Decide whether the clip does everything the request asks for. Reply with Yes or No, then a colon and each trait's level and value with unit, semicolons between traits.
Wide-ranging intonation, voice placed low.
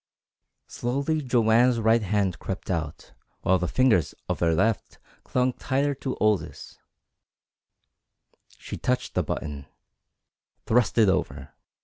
Yes: wide, 5.7 semitones; low, 110 Hz